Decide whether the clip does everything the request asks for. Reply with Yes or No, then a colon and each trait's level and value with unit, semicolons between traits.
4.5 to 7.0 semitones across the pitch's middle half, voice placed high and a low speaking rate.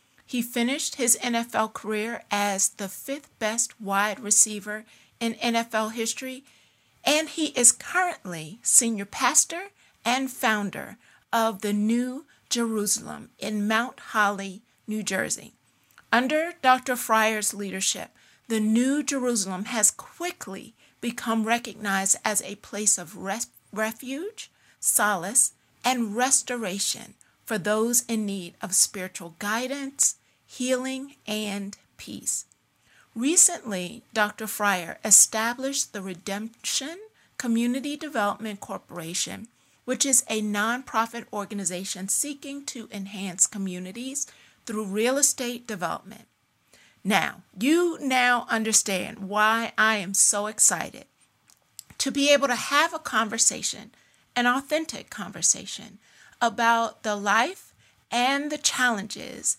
No: average, 3.7 semitones; high, 225 Hz; slow, 110 wpm